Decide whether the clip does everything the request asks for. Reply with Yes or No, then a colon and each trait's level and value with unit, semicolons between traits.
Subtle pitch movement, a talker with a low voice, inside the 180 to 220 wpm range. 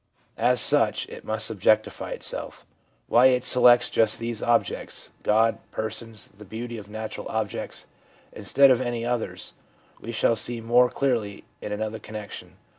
No: narrow, 1.9 semitones; low, 115 Hz; average, 155 wpm